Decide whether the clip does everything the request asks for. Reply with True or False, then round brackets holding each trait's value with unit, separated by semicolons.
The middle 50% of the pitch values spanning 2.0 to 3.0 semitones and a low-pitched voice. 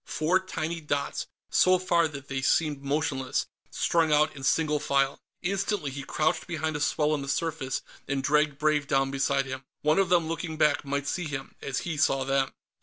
False (2.7 semitones; 150 Hz)